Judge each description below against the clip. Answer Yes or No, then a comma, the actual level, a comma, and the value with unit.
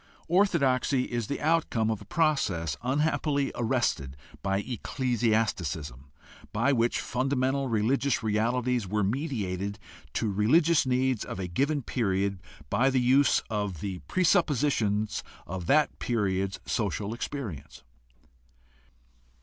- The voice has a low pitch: Yes, low, 115 Hz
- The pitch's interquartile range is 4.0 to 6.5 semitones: Yes, wide, 5.4 semitones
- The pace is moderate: No, slow, 110 wpm